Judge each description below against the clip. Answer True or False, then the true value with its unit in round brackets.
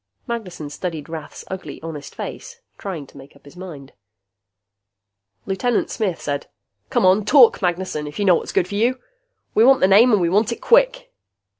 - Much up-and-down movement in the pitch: True (6.2 semitones)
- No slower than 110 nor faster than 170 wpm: False (180 wpm)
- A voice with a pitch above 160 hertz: True (190 Hz)